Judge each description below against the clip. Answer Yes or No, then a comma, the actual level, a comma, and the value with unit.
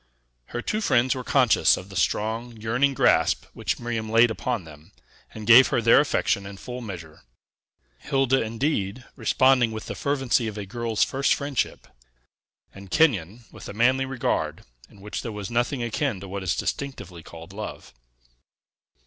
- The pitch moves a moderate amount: Yes, average, 4.4 semitones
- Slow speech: No, average, 165 wpm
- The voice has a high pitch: No, low, 115 Hz